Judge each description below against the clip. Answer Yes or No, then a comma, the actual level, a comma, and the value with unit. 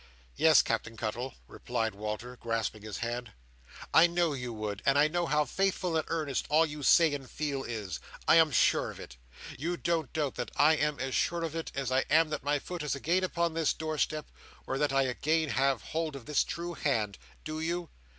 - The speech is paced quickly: Yes, fast, 210 wpm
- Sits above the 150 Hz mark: No, medium, 145 Hz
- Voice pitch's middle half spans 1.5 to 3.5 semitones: No, average, 4.6 semitones